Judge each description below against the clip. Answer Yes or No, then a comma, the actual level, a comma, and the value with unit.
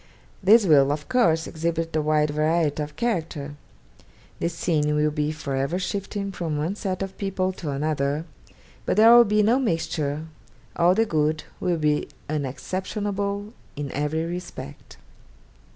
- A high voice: No, medium, 160 Hz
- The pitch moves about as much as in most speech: Yes, average, 4.5 semitones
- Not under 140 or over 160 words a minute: Yes, average, 150 wpm